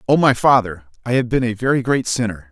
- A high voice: No, low, 115 Hz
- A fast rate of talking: Yes, fast, 240 wpm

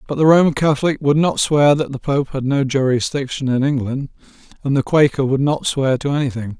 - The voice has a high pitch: No, medium, 140 Hz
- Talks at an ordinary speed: No, fast, 210 wpm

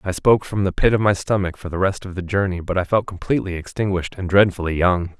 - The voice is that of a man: Yes, male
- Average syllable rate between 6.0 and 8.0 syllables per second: Yes, 6.5 syllables/s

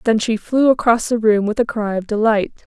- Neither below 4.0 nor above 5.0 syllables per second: No, 5.4 syllables/s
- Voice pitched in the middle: No, high, 220 Hz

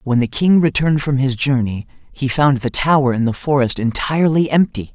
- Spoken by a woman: No, male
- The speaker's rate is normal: Yes, average, 195 wpm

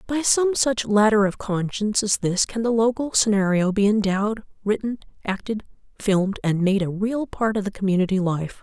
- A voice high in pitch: Yes, high, 210 Hz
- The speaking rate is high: No, average, 180 wpm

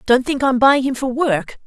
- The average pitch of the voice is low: No, very high, 255 Hz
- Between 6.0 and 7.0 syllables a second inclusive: No, 4.6 syllables/s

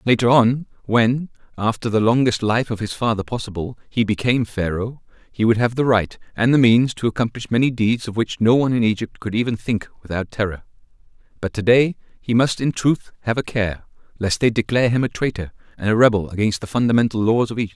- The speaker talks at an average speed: No, fast, 210 wpm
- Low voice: Yes, low, 115 Hz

